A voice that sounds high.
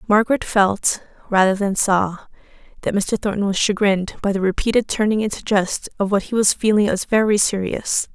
Yes: high, 205 Hz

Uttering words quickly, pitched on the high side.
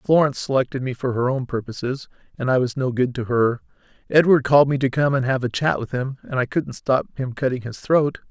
No: fast, 240 wpm; low, 130 Hz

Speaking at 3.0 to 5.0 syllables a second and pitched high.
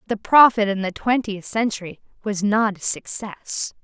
Yes: 4.5 syllables/s; high, 210 Hz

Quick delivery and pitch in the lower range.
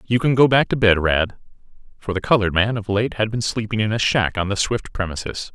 Yes: fast, 250 wpm; low, 105 Hz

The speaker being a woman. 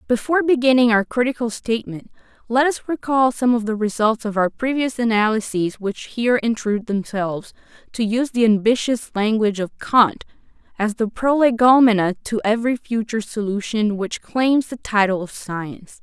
Yes: female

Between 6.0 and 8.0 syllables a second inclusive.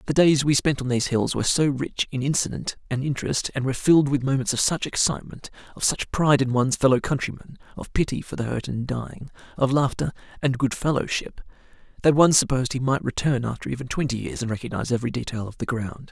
Yes: 6.5 syllables/s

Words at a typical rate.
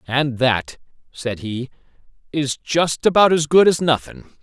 Yes: average, 150 wpm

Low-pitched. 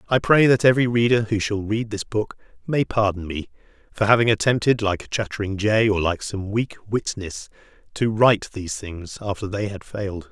Yes: low, 105 Hz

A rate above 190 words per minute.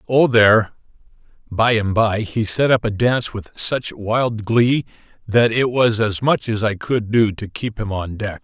Yes: average, 200 wpm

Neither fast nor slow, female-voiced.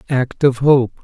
No: average, 175 wpm; male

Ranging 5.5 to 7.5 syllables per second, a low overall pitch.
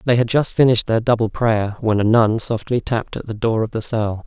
Yes: 5.6 syllables/s; low, 115 Hz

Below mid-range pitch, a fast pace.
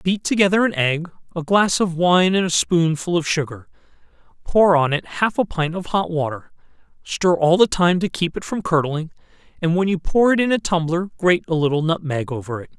No: medium, 170 Hz; fast, 210 wpm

